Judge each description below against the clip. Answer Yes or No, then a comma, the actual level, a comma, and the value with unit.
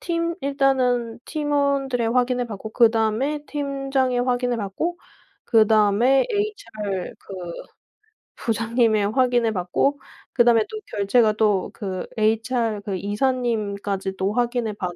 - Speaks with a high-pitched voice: Yes, high, 235 Hz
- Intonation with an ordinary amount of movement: Yes, average, 4.0 semitones